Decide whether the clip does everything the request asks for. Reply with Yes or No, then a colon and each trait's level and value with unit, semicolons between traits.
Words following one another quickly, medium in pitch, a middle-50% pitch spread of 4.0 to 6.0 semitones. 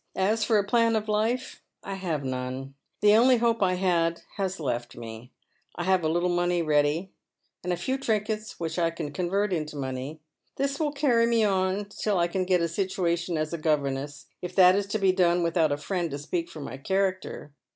Yes: fast, 210 wpm; medium, 180 Hz; average, 4.6 semitones